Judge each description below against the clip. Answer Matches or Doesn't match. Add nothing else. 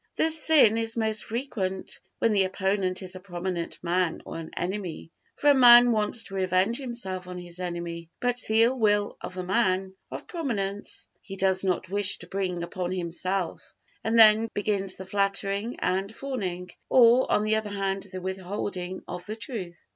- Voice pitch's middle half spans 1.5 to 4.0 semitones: Matches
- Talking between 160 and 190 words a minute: Matches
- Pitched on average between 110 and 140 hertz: Doesn't match